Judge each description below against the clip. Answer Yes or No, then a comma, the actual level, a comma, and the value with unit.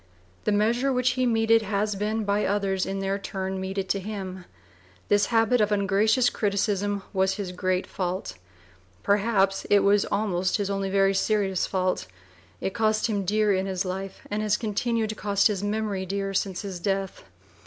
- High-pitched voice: Yes, high, 200 Hz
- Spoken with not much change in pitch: Yes, narrow, 1.9 semitones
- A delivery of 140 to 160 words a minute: No, average, 175 wpm